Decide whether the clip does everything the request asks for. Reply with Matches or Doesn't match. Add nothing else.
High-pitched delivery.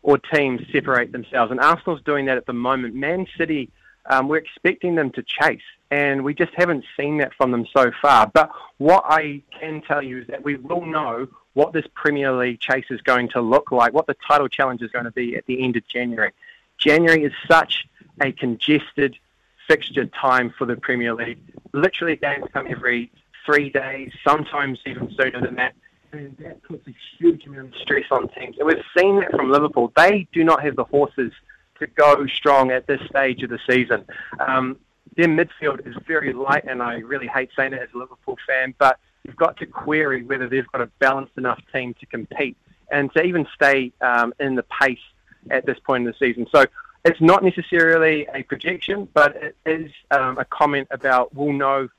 Doesn't match